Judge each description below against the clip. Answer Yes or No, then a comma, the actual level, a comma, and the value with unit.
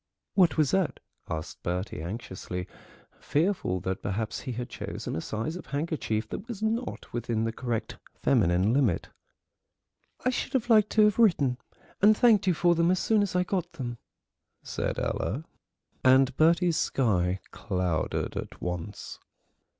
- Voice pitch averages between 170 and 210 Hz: No, low, 135 Hz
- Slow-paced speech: No, average, 150 wpm